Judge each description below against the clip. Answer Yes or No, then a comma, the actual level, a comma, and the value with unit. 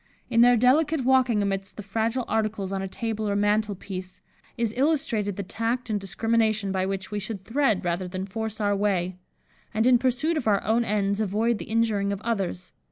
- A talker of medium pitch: No, high, 215 Hz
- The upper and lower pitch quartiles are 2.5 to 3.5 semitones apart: Yes, average, 2.9 semitones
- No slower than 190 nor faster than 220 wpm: Yes, average, 195 wpm